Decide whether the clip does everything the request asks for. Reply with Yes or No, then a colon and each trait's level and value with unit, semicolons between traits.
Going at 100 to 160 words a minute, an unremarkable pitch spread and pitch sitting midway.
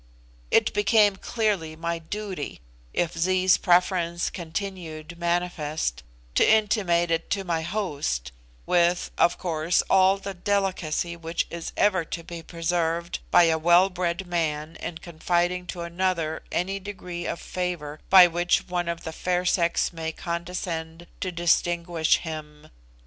No: average, 140 wpm; narrow, 1.9 semitones; medium, 175 Hz